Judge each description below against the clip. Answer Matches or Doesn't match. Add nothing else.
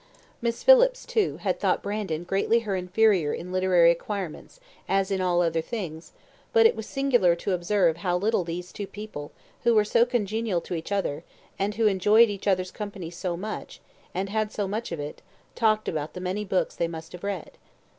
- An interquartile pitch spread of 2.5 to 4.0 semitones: Matches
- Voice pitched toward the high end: Matches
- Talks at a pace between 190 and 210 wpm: Matches